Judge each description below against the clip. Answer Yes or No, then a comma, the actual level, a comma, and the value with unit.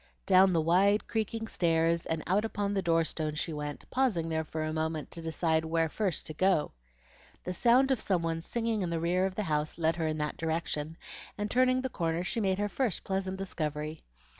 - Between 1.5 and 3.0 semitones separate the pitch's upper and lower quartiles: No, average, 3.9 semitones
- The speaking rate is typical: No, fast, 215 wpm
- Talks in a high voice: No, medium, 170 Hz